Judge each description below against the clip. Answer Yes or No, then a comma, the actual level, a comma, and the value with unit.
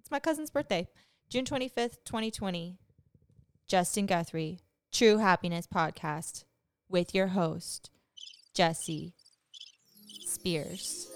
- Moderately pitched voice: Yes, medium, 180 Hz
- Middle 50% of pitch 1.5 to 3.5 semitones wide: No, average, 4.1 semitones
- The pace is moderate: No, slow, 90 wpm